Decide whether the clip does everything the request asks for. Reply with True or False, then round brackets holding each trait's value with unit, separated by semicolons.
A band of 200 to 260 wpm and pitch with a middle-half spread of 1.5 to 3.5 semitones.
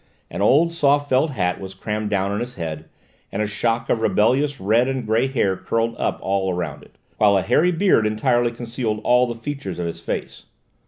False (205 wpm; 4.5 semitones)